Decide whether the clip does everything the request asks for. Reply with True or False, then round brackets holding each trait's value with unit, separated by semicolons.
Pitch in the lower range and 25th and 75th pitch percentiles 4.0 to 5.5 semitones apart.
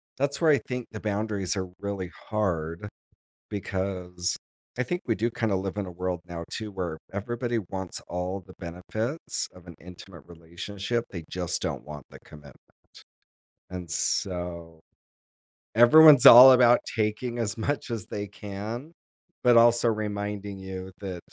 True (100 Hz; 4.4 semitones)